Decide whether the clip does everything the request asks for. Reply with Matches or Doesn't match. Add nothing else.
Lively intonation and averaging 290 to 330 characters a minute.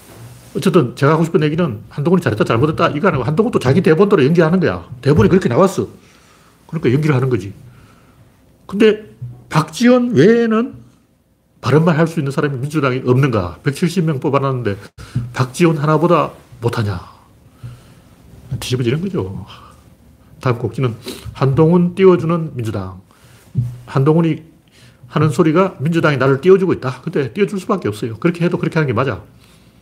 Doesn't match